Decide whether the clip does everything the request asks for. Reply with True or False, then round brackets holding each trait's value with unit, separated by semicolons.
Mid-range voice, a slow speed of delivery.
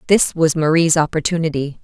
True (160 Hz; 130 wpm)